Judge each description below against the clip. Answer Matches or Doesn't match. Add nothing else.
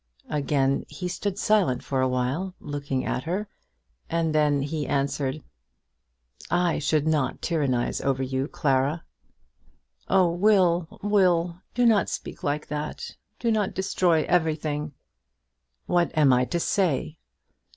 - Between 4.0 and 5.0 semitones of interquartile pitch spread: Matches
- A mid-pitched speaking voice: Matches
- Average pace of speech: Doesn't match